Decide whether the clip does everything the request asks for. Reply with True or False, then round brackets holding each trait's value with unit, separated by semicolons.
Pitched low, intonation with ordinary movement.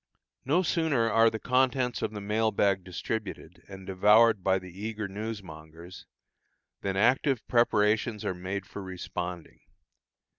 True (105 Hz; 3.4 semitones)